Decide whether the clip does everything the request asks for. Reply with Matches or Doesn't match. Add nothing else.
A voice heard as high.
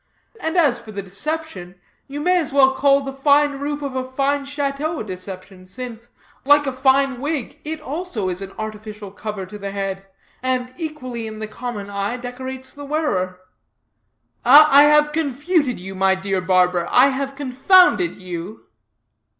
Matches